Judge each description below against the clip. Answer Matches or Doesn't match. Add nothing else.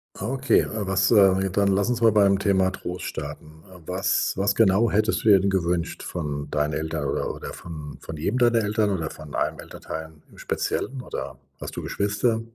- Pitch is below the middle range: Matches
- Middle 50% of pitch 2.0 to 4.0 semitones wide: Doesn't match